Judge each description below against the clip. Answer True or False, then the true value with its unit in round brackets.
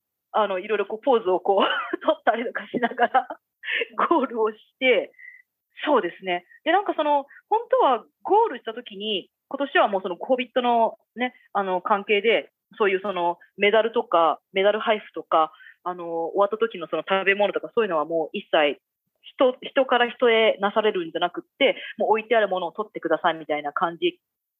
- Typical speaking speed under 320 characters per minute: False (355 characters per minute)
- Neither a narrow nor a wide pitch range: False (7.6 semitones)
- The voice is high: True (220 Hz)